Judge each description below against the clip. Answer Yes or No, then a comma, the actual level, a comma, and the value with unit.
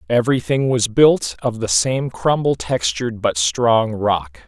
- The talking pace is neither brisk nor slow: Yes, average, 145 wpm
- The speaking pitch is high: No, low, 115 Hz